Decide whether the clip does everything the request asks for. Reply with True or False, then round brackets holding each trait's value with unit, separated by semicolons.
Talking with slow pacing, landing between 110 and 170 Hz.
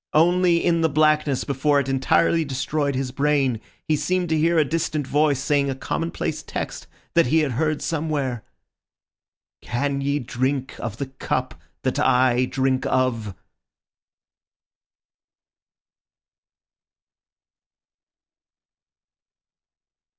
True (105 wpm; 140 Hz)